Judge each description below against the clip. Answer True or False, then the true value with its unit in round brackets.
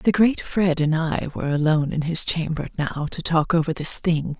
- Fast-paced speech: True (220 wpm)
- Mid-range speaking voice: True (160 Hz)